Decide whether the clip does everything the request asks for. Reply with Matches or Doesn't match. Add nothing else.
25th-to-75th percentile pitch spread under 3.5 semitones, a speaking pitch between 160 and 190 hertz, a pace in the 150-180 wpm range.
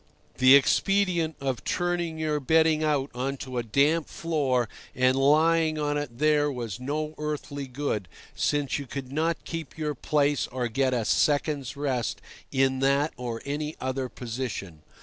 Doesn't match